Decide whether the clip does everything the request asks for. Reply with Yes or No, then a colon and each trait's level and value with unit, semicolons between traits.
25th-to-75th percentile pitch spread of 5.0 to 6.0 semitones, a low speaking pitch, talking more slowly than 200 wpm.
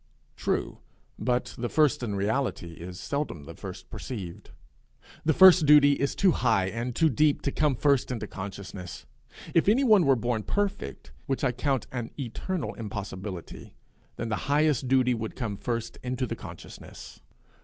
Yes: average, 5.3 semitones; low, 125 Hz; average, 160 wpm